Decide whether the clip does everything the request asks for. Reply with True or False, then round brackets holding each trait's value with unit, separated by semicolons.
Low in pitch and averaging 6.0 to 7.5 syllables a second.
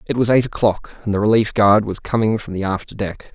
False (105 Hz; 5.8 syllables/s)